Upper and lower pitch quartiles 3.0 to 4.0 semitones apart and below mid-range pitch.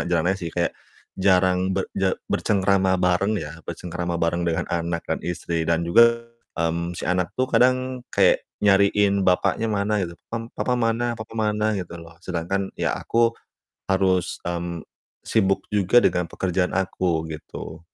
Yes: average, 3.3 semitones; very low, 95 Hz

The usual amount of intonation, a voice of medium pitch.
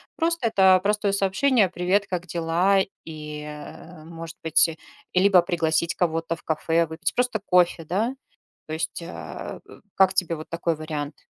Yes: average, 3.0 semitones; medium, 175 Hz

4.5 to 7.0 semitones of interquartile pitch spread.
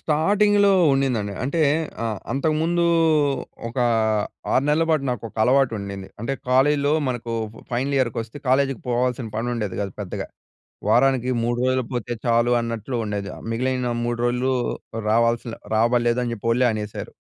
No: average, 2.8 semitones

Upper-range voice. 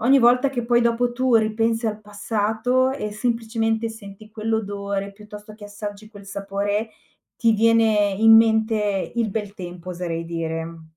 Yes: high, 215 Hz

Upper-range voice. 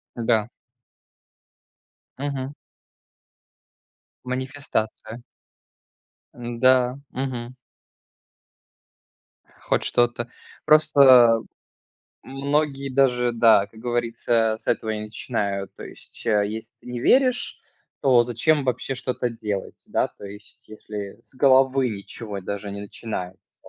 No: low, 120 Hz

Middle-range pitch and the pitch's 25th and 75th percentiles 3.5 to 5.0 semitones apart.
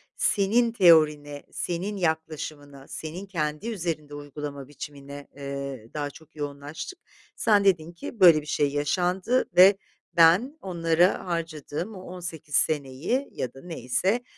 Yes: medium, 160 Hz; average, 4.1 semitones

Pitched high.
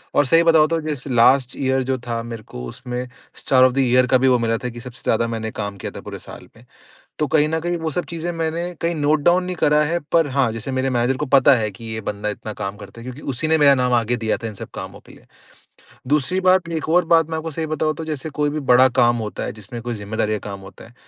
No: low, 130 Hz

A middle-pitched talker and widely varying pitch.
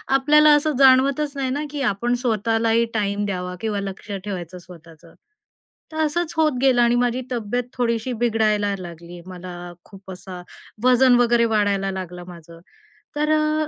No: high, 225 Hz; wide, 5.7 semitones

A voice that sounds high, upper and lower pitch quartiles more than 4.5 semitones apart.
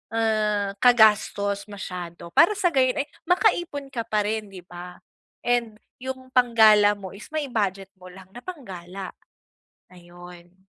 Yes: high, 210 Hz; average, 5.0 semitones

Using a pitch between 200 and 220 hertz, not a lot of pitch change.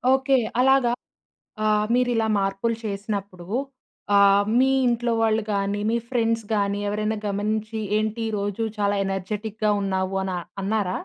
Yes: high, 210 Hz; narrow, 2.2 semitones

